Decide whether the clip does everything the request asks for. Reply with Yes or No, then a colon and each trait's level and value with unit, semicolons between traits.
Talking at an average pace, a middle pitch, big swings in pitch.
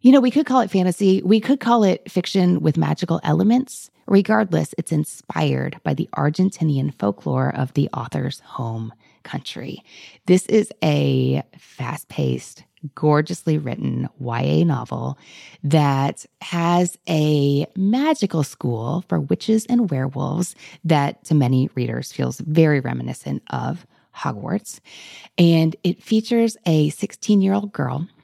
No: slow, 130 wpm; medium, 160 Hz; wide, 6.2 semitones